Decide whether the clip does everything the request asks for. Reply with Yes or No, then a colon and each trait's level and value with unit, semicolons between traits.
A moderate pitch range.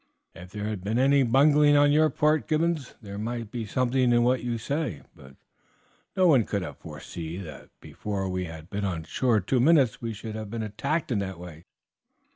No: wide, 5.8 semitones